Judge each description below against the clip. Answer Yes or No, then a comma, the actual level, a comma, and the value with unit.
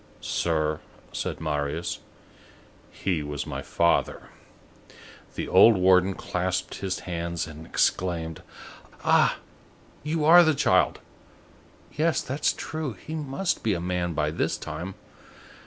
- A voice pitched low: Yes, very low, 90 Hz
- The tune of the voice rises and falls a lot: Yes, wide, 8.6 semitones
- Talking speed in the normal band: No, slow, 120 wpm